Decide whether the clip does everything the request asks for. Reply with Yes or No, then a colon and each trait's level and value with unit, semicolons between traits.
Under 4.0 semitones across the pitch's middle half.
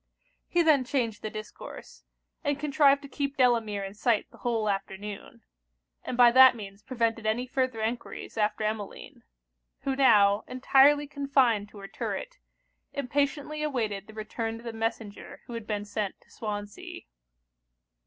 No: average, 4.4 semitones